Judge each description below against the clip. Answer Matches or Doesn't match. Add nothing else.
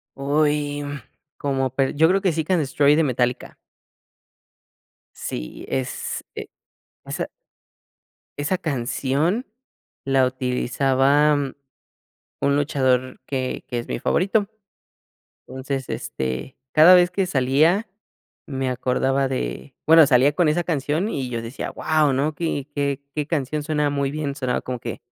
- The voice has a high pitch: Doesn't match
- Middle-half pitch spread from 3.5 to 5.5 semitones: Doesn't match